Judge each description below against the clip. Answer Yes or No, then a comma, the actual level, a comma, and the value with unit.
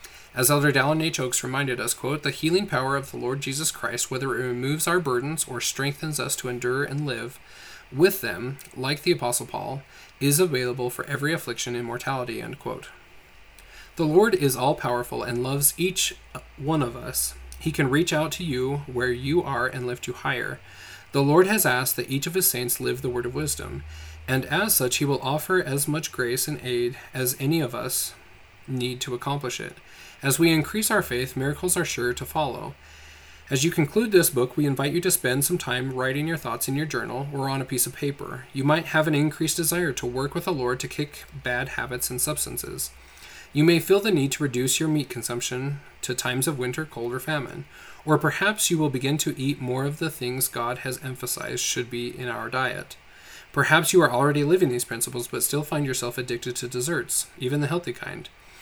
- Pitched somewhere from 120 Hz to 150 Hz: Yes, low, 135 Hz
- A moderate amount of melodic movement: Yes, average, 3.7 semitones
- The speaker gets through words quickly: Yes, fast, 210 wpm